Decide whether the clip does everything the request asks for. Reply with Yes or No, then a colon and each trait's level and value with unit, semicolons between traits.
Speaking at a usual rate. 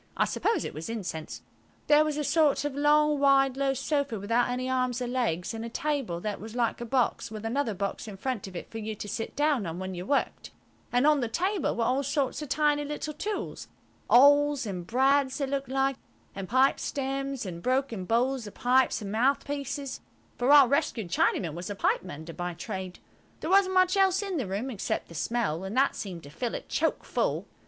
No: fast, 210 wpm